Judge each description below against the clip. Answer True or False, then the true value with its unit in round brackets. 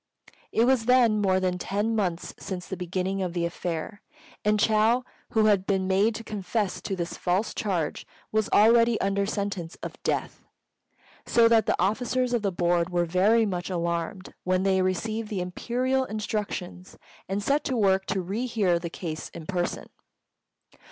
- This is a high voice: True (195 Hz)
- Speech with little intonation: False (3.4 semitones)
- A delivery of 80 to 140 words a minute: False (170 wpm)